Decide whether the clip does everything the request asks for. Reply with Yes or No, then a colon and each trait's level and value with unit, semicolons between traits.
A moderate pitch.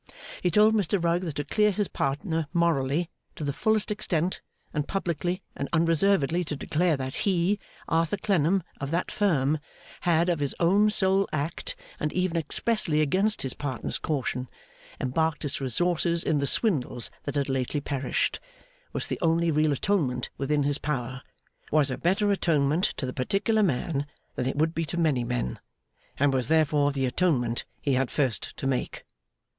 Yes: medium, 155 Hz